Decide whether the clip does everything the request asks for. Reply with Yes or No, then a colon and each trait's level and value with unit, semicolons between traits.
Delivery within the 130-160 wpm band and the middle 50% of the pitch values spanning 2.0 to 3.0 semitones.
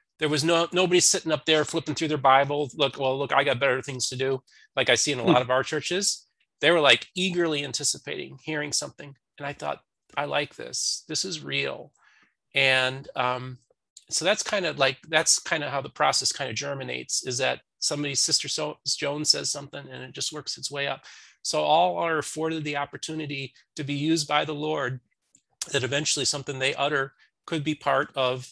No: fast, 205 wpm; narrow, 2.4 semitones